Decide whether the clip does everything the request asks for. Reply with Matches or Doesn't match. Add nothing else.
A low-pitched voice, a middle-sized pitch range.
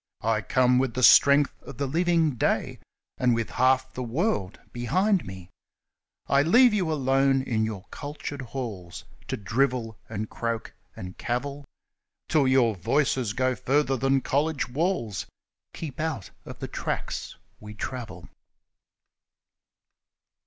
Matches